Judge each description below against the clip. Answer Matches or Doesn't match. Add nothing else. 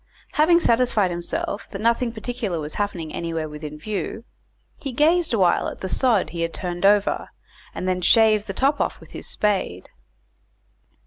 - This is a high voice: Matches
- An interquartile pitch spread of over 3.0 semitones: Matches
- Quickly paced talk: Doesn't match